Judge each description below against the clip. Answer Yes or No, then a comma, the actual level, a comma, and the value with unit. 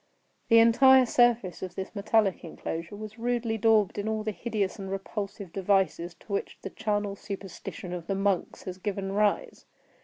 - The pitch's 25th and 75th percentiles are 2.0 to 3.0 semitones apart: Yes, narrow, 2.6 semitones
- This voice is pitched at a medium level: No, high, 200 Hz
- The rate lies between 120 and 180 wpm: Yes, average, 165 wpm